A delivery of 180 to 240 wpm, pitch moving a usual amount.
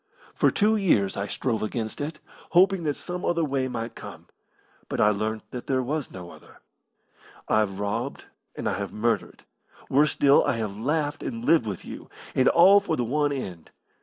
No: average, 185 wpm; wide, 6.2 semitones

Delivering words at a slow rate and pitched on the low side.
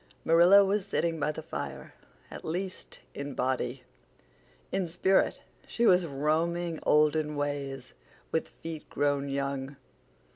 No: slow, 115 wpm; medium, 150 Hz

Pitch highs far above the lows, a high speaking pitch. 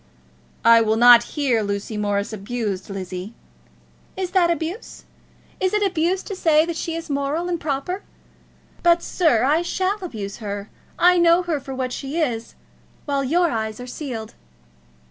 Yes: wide, 7.4 semitones; very high, 280 Hz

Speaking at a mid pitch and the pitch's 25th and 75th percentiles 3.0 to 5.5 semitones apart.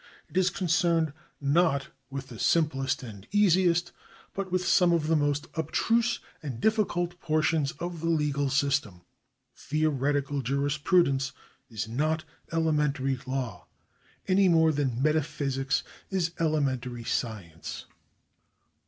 Yes: medium, 150 Hz; average, 4.0 semitones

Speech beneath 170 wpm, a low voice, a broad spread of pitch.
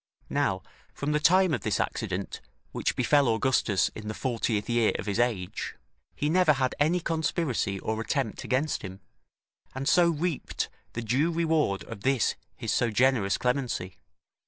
Yes: average, 160 wpm; low, 130 Hz; wide, 5.8 semitones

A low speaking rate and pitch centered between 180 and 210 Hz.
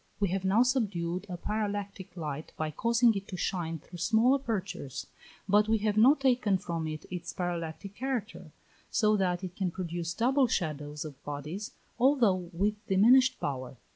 No: average, 165 wpm; high, 190 Hz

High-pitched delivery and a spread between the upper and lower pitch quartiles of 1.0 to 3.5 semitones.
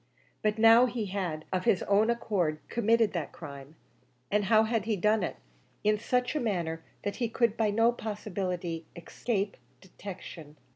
No: high, 205 Hz; average, 4.2 semitones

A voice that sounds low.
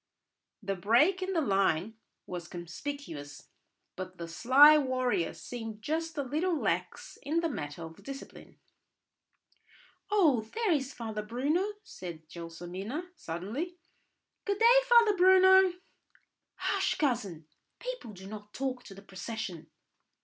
No: high, 245 Hz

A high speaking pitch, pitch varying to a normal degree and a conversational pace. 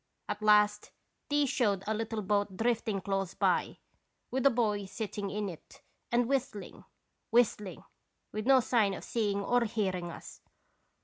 Yes: high, 210 Hz; average, 3.0 semitones; average, 145 wpm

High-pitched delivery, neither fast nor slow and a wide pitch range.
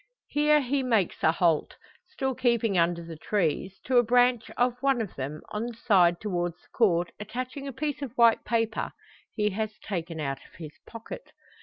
Yes: high, 220 Hz; average, 185 wpm; wide, 6.1 semitones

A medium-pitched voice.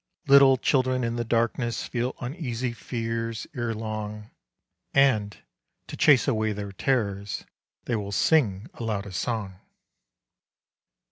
No: low, 115 Hz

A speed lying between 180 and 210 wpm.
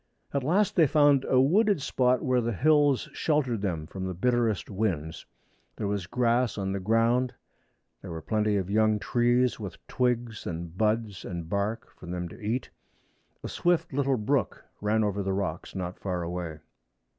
No: average, 170 wpm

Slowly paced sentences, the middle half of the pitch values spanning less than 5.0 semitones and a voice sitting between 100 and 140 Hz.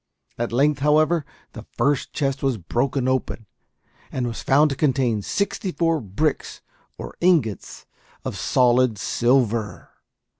Yes: slow, 125 wpm; average, 3.9 semitones; low, 135 Hz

